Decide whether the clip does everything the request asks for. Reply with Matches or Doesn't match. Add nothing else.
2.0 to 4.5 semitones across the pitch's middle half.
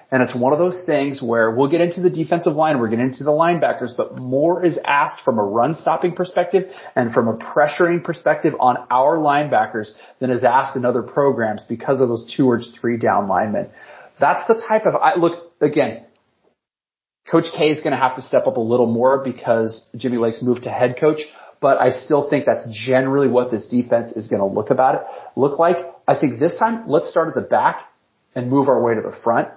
Doesn't match